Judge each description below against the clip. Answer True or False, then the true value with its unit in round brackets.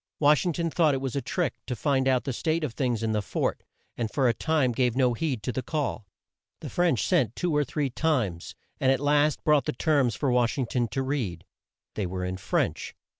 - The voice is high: False (130 Hz)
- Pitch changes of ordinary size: True (4.0 semitones)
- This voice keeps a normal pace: False (230 wpm)